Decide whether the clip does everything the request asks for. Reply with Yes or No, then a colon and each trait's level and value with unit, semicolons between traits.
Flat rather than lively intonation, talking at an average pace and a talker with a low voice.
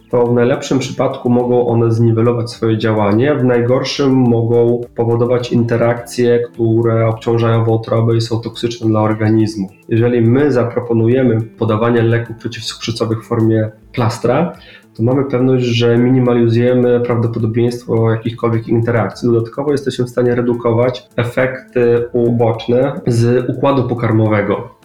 Yes: narrow, 1.2 semitones; average, 120 wpm; low, 120 Hz